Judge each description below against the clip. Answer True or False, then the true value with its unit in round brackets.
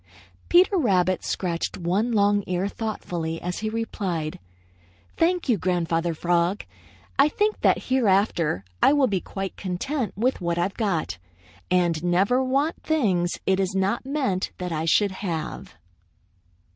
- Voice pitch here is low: False (190 Hz)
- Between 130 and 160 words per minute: True (140 wpm)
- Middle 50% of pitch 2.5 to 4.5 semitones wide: False (5.2 semitones)